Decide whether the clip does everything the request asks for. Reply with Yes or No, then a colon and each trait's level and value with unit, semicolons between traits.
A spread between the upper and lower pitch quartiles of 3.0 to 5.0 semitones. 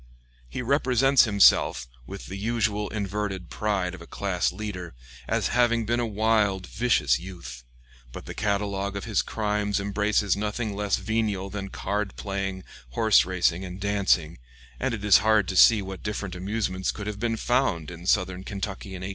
No: narrow, 2.4 semitones